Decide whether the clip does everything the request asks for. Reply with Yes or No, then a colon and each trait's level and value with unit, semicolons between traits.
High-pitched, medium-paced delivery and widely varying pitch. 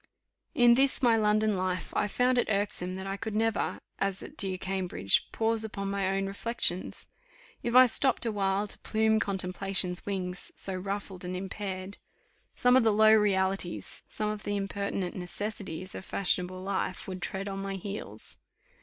No: high, 195 Hz; average, 165 wpm; narrow, 2.4 semitones